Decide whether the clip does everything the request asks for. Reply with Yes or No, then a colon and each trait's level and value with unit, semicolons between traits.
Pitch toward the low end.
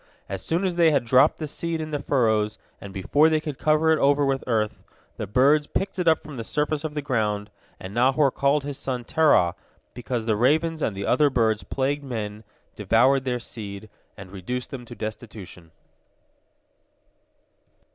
Yes: low, 130 Hz